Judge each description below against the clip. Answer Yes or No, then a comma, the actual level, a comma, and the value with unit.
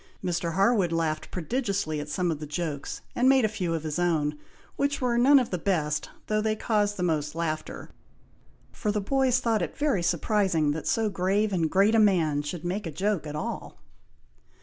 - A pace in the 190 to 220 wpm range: Yes, average, 195 wpm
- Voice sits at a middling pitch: Yes, medium, 180 Hz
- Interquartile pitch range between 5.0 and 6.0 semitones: Yes, average, 5.3 semitones